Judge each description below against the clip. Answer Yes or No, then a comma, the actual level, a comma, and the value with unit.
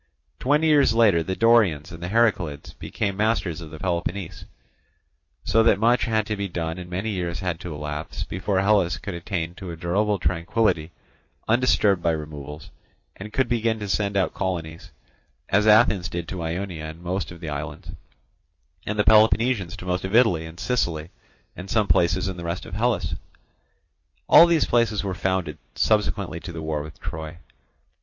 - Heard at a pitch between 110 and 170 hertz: No, very low, 95 Hz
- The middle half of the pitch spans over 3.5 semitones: Yes, average, 4.3 semitones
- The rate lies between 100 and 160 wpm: No, average, 175 wpm